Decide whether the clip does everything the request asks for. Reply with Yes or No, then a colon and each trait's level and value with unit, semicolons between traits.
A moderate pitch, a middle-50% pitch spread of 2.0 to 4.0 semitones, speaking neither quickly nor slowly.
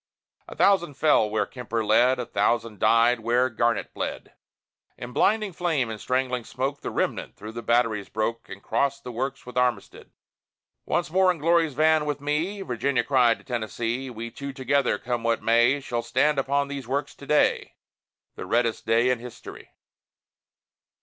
No: low, 125 Hz; average, 3.4 semitones; average, 170 wpm